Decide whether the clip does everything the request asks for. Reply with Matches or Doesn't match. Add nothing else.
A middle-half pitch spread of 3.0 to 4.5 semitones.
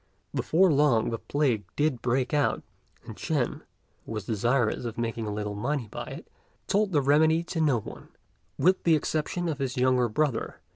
Doesn't match